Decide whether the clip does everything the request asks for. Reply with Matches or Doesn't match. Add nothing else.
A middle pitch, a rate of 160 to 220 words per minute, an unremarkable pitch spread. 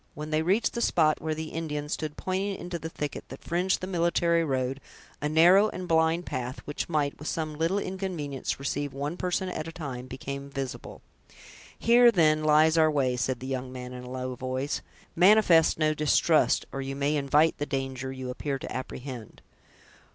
Matches